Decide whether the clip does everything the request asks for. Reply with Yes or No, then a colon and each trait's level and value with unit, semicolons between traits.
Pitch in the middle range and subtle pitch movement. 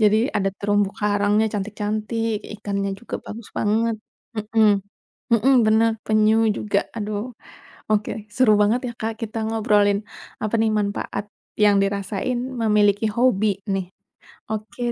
No: high, 215 Hz; narrow, 1.6 semitones